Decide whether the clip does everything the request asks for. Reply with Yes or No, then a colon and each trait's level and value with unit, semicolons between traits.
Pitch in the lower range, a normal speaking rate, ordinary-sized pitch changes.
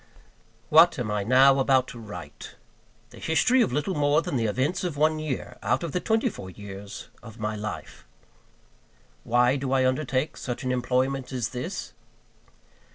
Yes: low, 130 Hz; average, 165 wpm; average, 4.6 semitones